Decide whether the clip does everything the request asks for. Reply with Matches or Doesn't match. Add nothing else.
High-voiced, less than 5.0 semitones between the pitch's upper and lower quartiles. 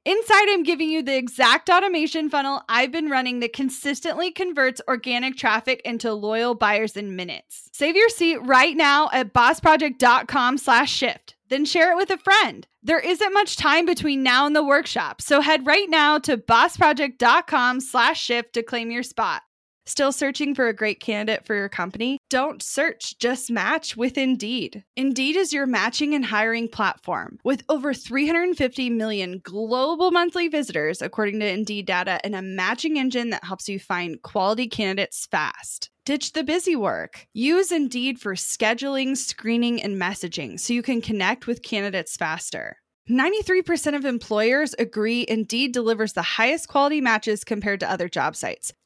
Doesn't match